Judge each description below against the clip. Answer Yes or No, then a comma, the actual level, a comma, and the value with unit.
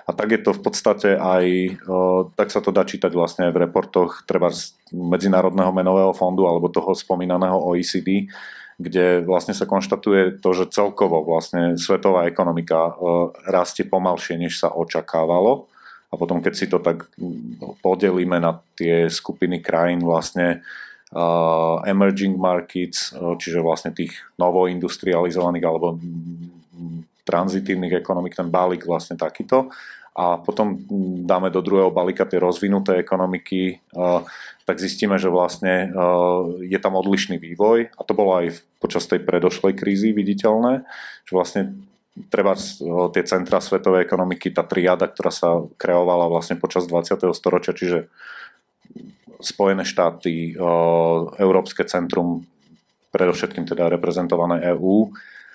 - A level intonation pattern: Yes, narrow, 1.7 semitones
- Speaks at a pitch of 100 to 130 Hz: No, very low, 90 Hz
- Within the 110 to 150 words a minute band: Yes, average, 130 wpm